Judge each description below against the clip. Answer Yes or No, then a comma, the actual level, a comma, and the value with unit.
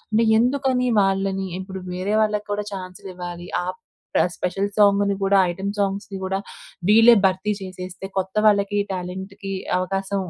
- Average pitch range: No, narrow, 1.6 semitones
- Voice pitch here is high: Yes, high, 195 Hz